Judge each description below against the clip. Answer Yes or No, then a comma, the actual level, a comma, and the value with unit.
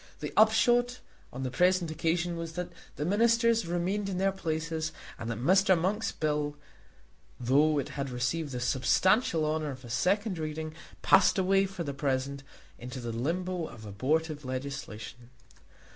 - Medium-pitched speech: Yes, medium, 160 Hz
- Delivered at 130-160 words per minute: Yes, average, 155 wpm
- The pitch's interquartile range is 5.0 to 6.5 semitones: Yes, wide, 5.6 semitones